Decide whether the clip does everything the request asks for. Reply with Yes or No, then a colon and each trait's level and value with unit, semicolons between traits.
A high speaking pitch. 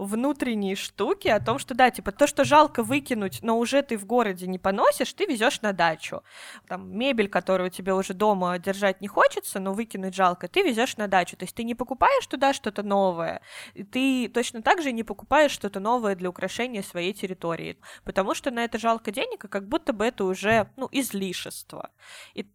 Yes: high, 220 Hz